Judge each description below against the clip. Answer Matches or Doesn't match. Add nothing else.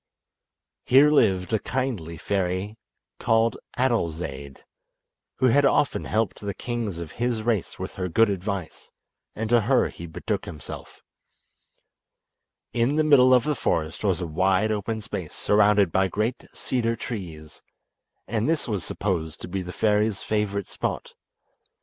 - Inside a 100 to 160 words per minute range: Matches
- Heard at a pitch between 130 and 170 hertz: Doesn't match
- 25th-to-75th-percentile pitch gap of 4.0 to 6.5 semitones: Matches